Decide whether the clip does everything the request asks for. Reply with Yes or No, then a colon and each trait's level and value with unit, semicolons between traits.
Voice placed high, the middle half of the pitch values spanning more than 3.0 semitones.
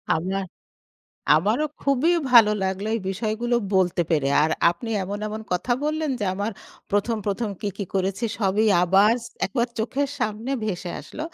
Yes: high, 210 Hz; average, 3.7 semitones